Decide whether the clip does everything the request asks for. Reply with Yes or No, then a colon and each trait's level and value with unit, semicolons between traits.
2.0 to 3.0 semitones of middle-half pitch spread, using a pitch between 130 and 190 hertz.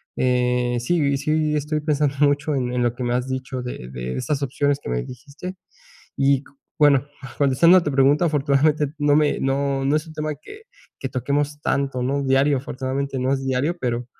Yes: narrow, 2.5 semitones; medium, 140 Hz